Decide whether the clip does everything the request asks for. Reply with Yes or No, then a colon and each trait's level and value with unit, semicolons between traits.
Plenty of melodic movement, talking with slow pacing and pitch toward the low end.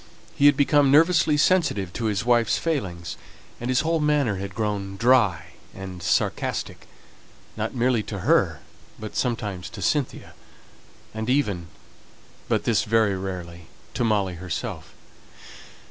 Yes: wide, 6.1 semitones; slow, 130 wpm; low, 110 Hz